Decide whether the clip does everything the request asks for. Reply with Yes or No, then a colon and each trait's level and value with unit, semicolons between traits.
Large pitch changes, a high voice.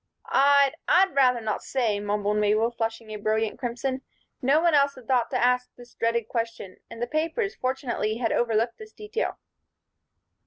No: average, 3.7 semitones; high, 240 Hz